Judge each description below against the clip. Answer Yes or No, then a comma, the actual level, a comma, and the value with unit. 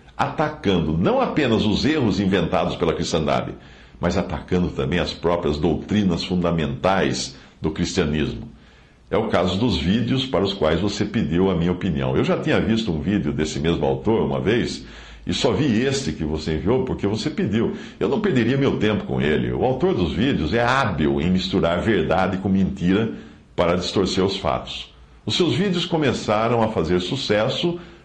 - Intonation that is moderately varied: No, wide, 5.7 semitones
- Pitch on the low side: Yes, very low, 90 Hz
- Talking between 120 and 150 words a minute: No, average, 170 wpm